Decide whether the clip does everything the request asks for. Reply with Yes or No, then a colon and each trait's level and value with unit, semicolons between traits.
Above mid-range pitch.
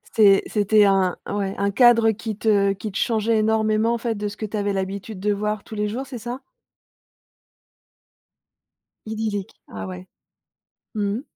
Yes: high, 210 Hz